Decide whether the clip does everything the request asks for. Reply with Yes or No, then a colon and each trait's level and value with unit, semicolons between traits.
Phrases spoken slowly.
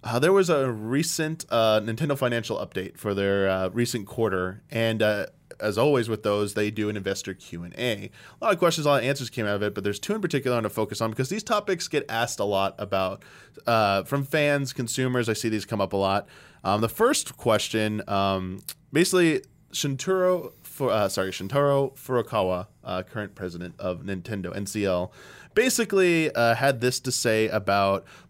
No: average, 195 wpm